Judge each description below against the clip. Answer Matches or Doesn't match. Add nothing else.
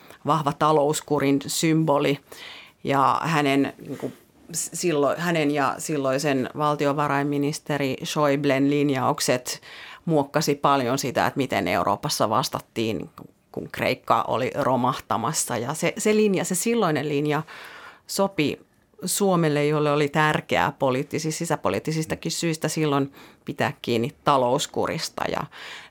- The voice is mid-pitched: Matches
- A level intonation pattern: Matches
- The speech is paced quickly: Doesn't match